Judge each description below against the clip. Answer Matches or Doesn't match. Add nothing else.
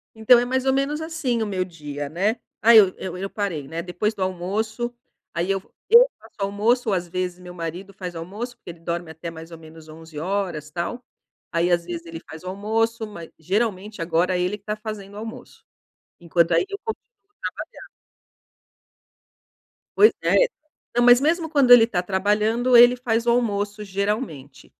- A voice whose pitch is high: Matches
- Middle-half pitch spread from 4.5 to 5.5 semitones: Matches